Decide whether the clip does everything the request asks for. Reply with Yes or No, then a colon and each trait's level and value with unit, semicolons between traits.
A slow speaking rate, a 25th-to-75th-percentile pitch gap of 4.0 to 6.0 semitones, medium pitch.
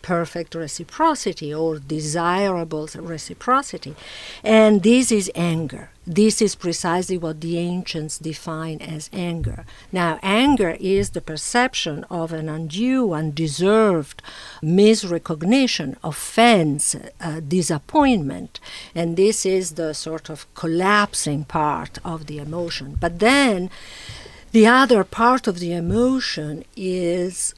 Yes: slow, 110 wpm; average, 4.7 semitones; medium, 170 Hz